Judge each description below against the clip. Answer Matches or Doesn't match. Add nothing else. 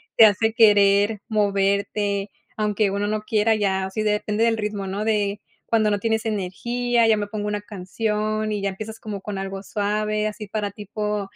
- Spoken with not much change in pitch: Matches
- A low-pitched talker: Doesn't match